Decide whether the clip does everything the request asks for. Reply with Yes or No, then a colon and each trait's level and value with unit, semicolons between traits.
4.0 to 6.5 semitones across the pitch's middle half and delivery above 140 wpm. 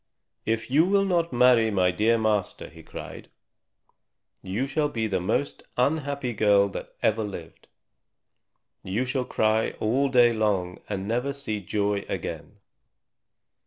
No: average, 4.7 semitones; slow, 135 wpm